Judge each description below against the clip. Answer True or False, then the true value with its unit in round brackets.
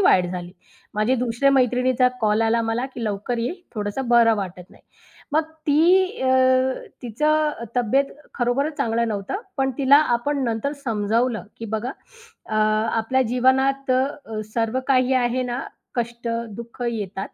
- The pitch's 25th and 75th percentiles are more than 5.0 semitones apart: False (3.0 semitones)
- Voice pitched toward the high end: True (240 Hz)